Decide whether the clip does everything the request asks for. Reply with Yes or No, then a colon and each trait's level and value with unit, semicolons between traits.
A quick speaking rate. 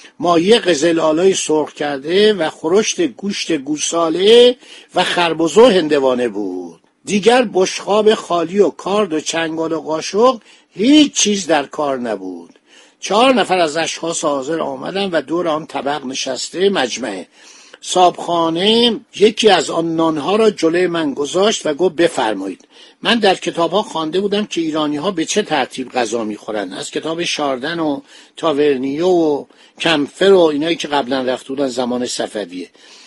No: average, 140 wpm